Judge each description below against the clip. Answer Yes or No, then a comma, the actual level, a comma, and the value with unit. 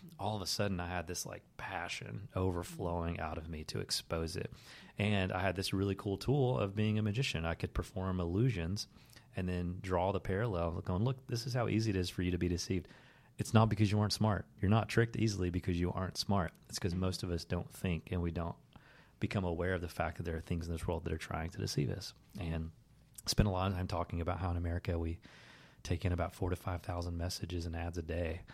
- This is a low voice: Yes, very low, 95 Hz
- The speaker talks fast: Yes, fast, 245 wpm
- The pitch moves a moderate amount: Yes, average, 3.4 semitones